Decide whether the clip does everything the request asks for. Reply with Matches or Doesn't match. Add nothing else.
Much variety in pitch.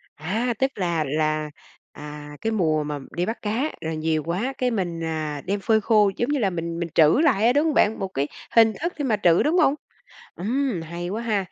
Matches